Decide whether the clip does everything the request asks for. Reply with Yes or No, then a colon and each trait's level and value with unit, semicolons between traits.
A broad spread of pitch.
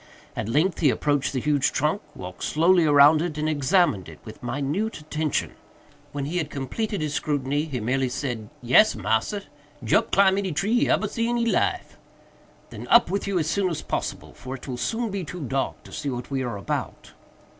Yes: wide, 6.1 semitones